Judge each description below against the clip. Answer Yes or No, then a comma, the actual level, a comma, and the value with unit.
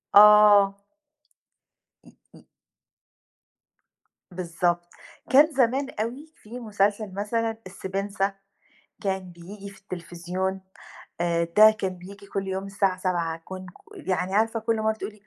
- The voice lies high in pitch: Yes, high, 195 Hz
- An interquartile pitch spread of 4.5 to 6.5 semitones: No, average, 2.8 semitones